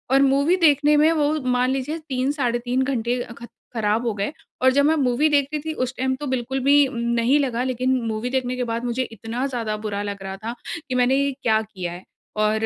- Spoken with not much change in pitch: No, average, 3.1 semitones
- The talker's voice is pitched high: Yes, very high, 255 Hz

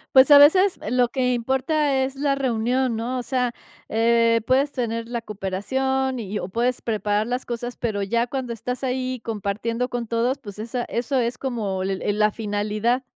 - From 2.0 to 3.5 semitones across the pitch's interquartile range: Yes, average, 2.8 semitones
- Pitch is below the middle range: No, high, 240 Hz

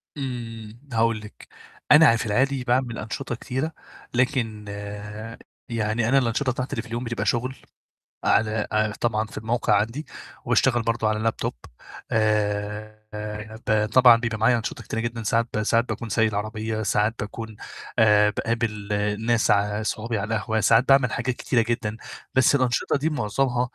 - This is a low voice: Yes, low, 115 Hz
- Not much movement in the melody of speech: Yes, narrow, 2.1 semitones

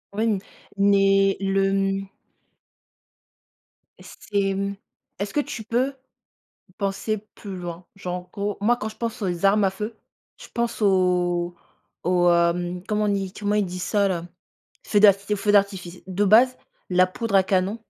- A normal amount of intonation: No, narrow, 2.3 semitones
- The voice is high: Yes, high, 195 Hz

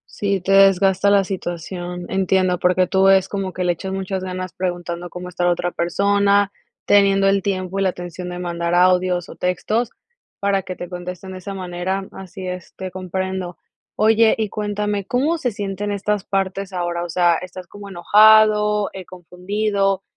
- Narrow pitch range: Yes, narrow, 1.9 semitones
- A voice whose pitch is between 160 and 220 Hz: Yes, high, 190 Hz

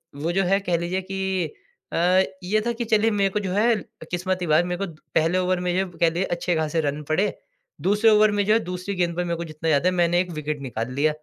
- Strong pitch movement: No, average, 2.8 semitones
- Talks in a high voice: No, medium, 180 Hz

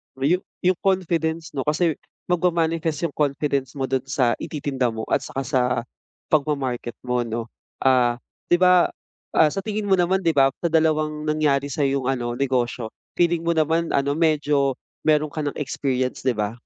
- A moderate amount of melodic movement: Yes, average, 3.7 semitones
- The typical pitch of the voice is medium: Yes, medium, 145 Hz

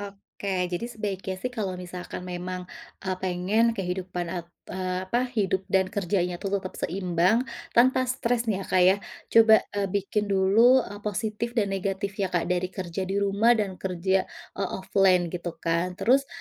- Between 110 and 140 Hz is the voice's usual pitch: No, high, 190 Hz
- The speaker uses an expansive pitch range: No, narrow, 2.4 semitones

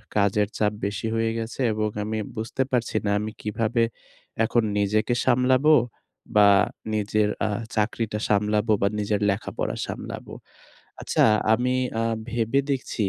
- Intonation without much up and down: Yes, narrow, 2.0 semitones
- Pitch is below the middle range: Yes, low, 110 Hz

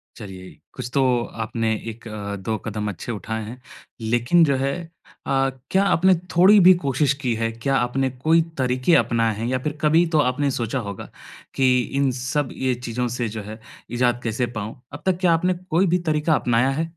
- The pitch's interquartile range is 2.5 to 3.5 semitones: No, average, 4.8 semitones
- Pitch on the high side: No, low, 125 Hz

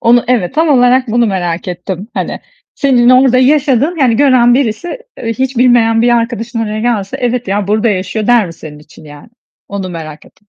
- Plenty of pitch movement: No, average, 4.3 semitones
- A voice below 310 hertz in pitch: Yes, high, 230 Hz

